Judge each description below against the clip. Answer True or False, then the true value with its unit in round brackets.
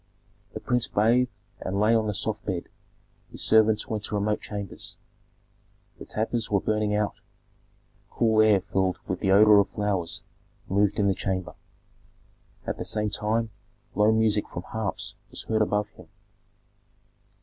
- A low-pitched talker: True (105 Hz)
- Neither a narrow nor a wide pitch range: False (1.5 semitones)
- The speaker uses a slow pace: False (150 wpm)